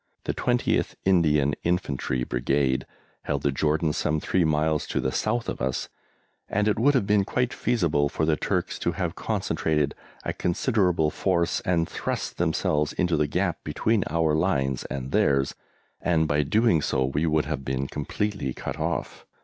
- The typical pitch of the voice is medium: No, very low, 80 Hz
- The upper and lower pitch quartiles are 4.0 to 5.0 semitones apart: Yes, average, 4.4 semitones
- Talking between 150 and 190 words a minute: Yes, average, 165 wpm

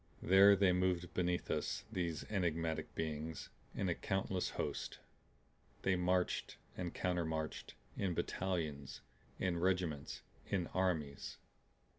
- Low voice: Yes, very low, 90 Hz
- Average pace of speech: No, slow, 110 wpm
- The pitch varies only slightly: Yes, narrow, 2.3 semitones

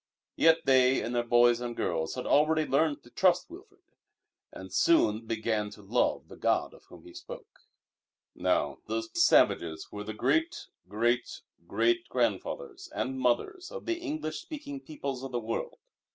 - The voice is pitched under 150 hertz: Yes, medium, 140 Hz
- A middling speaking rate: Yes, average, 160 wpm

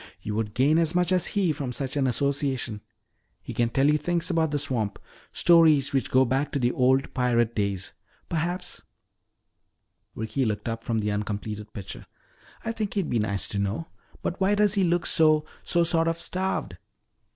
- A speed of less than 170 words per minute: No, average, 185 wpm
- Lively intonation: Yes, wide, 6.7 semitones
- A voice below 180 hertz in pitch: Yes, medium, 140 Hz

